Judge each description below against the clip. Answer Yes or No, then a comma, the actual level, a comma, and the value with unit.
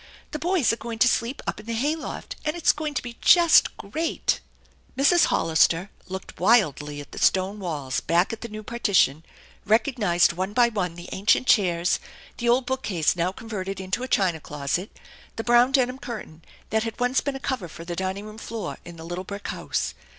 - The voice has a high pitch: Yes, high, 210 Hz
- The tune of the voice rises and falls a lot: Yes, wide, 5.8 semitones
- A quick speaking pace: Yes, fast, 210 wpm